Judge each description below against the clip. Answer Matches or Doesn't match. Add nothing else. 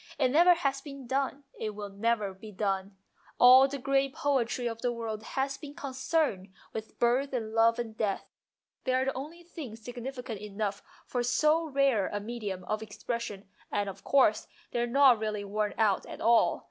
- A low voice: Doesn't match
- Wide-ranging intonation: Doesn't match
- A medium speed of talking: Matches